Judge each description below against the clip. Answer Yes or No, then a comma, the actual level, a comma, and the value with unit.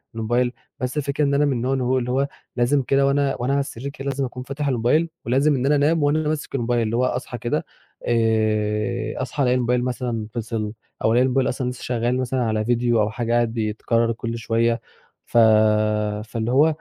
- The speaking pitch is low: Yes, low, 125 Hz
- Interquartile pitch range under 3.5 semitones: Yes, average, 2.9 semitones